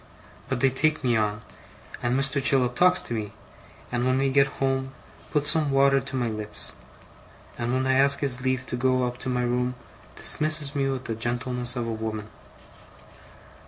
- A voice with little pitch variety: Yes, narrow, 2.0 semitones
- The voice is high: No, low, 130 Hz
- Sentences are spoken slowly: No, average, 185 wpm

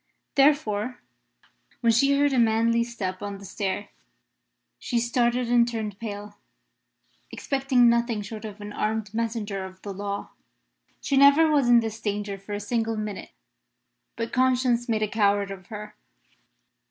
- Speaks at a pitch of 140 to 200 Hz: No, high, 225 Hz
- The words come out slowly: No, average, 150 wpm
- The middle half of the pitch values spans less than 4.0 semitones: Yes, average, 2.8 semitones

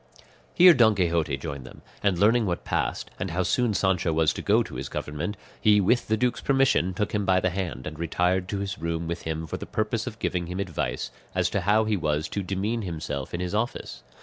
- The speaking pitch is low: Yes, very low, 95 Hz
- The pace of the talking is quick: Yes, fast, 230 wpm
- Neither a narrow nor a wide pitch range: Yes, average, 4.1 semitones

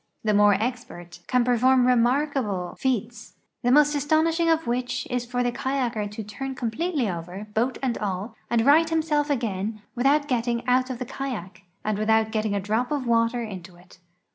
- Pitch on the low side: No, high, 240 Hz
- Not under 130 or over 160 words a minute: No, average, 185 wpm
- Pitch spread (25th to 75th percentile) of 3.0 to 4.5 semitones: Yes, average, 3.8 semitones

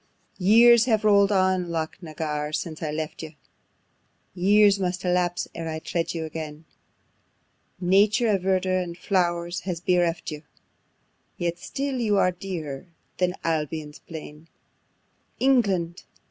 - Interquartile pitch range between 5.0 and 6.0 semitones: No, average, 3.3 semitones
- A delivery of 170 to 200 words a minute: No, slow, 135 wpm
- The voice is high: No, medium, 180 Hz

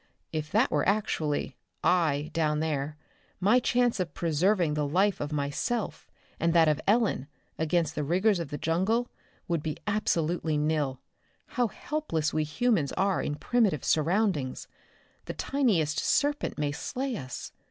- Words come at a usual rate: Yes, average, 145 wpm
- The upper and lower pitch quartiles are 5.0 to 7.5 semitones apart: Yes, wide, 5.6 semitones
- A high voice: No, medium, 165 Hz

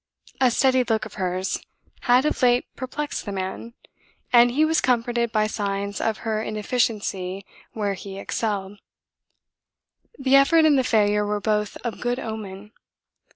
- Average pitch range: Yes, average, 3.5 semitones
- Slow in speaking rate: No, average, 150 wpm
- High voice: Yes, high, 220 Hz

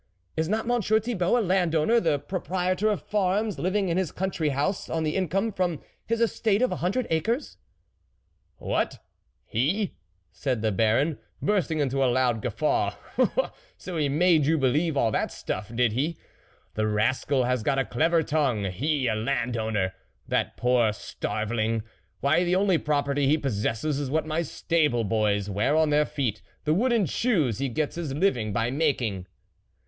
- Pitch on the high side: No, medium, 150 Hz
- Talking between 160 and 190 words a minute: Yes, average, 180 wpm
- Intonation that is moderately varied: No, wide, 7.0 semitones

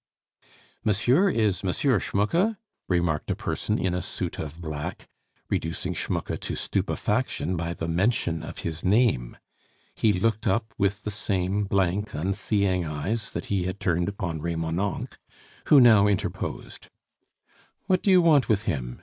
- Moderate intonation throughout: Yes, average, 4.4 semitones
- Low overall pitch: Yes, very low, 95 Hz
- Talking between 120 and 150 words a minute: Yes, average, 145 wpm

